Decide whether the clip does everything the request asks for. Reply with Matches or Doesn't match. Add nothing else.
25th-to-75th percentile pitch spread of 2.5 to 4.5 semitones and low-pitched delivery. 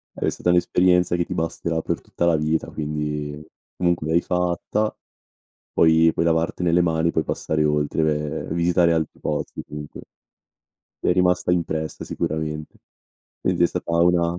Doesn't match